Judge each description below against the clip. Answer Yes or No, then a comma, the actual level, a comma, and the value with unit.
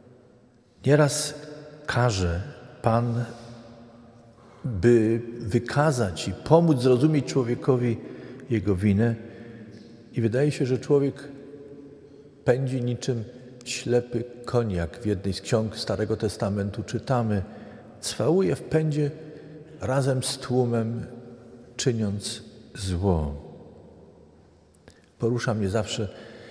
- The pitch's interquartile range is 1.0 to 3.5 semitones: Yes, average, 3.1 semitones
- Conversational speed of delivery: No, slow, 85 wpm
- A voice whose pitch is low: Yes, low, 120 Hz